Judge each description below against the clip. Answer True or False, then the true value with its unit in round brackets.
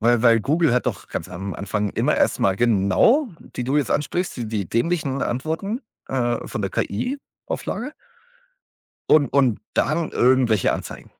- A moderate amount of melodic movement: False (6.0 semitones)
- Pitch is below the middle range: True (125 Hz)